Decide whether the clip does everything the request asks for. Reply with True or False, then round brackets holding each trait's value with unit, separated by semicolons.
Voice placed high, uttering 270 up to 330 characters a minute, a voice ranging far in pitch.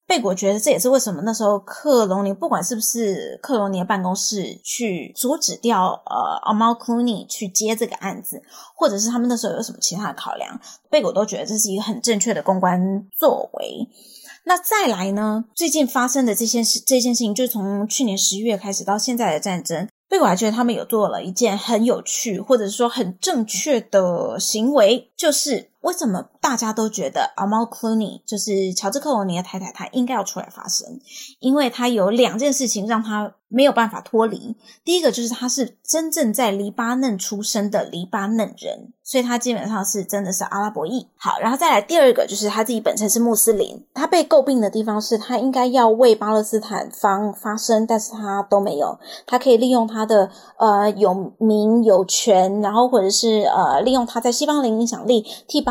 False (225 Hz; 310 characters per minute; 3.3 semitones)